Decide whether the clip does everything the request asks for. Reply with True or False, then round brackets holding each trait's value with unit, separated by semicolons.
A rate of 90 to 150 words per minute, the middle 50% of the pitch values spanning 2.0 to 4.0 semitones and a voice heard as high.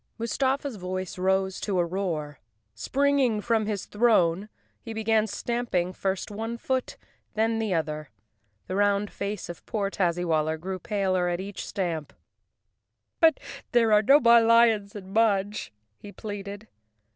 True (140 wpm; 3.5 semitones; 205 Hz)